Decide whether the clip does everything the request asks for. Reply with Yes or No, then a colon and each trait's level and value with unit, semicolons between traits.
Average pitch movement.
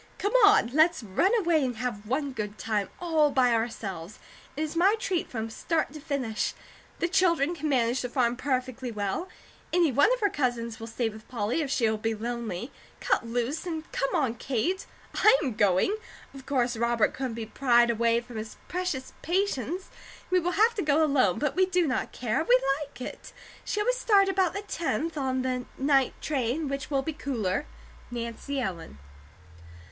No: wide, 5.7 semitones